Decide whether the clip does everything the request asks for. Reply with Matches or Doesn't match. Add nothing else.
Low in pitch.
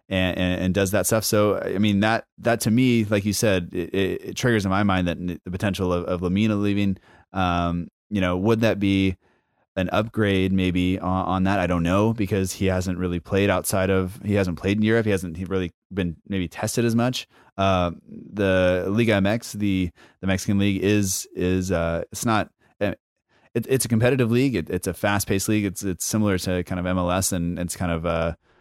Matches